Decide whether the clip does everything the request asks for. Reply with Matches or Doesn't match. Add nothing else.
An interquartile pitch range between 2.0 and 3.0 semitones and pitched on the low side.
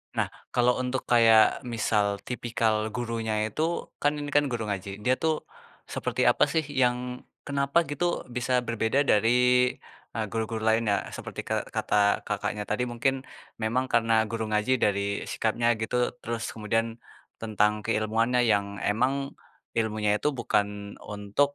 Matches